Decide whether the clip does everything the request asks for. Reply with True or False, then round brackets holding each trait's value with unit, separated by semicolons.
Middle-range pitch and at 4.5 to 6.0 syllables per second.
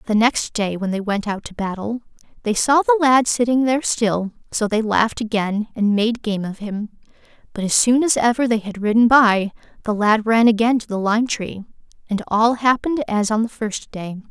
False (220 Hz; 5.1 syllables/s)